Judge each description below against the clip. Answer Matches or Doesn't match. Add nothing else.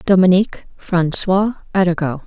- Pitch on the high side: Doesn't match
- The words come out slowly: Matches